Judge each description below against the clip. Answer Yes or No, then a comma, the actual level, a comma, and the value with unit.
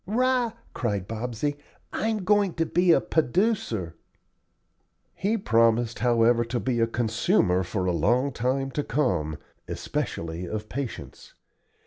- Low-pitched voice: Yes, low, 120 Hz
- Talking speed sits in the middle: No, slow, 125 wpm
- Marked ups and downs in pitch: Yes, wide, 7.4 semitones